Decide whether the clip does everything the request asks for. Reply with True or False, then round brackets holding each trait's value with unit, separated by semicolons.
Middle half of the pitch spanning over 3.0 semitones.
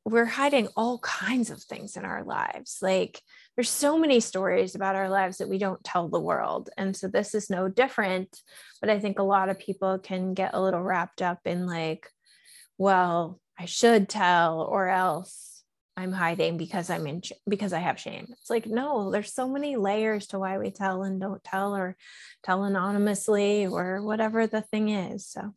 False (2.7 semitones)